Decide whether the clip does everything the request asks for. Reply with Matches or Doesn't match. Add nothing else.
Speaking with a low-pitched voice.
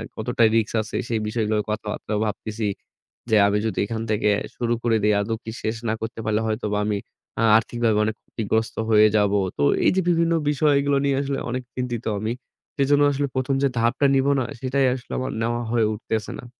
Matches